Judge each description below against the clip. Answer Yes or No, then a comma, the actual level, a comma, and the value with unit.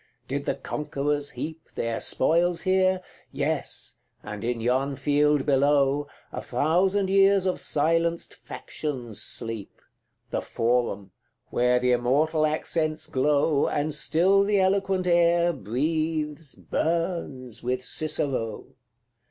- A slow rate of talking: Yes, slow, 110 wpm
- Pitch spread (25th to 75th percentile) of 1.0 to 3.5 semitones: No, average, 4.8 semitones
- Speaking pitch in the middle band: Yes, medium, 150 Hz